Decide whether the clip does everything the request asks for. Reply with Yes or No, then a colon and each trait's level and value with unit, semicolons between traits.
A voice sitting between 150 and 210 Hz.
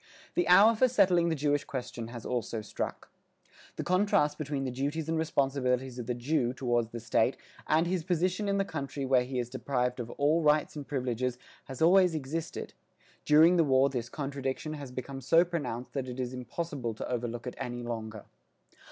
No: low, 135 Hz